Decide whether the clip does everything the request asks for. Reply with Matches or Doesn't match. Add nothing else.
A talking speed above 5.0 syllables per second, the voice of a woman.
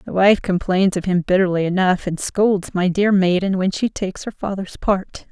Doesn't match